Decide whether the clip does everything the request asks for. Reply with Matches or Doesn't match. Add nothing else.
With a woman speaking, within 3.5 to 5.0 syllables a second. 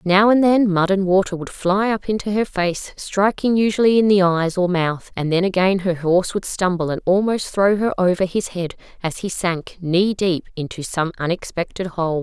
Matches